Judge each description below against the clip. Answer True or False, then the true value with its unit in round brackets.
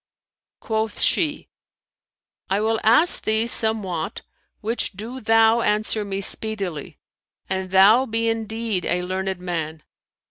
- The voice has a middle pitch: False (215 Hz)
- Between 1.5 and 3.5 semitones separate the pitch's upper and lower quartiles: True (3.0 semitones)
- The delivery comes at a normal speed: False (115 wpm)